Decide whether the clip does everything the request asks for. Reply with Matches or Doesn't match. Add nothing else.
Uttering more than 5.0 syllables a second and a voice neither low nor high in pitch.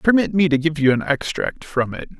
Matches